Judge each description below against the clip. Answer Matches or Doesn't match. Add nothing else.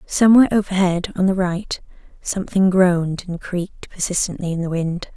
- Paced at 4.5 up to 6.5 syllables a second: Matches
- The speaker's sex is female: Matches